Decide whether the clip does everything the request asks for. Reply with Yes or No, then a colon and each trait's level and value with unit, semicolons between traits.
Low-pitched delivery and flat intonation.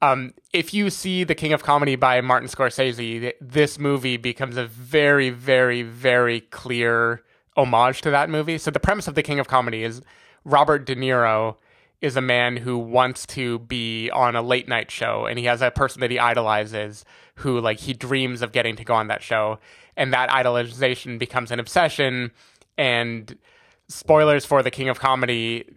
Yes: low, 125 Hz; narrow, 2.3 semitones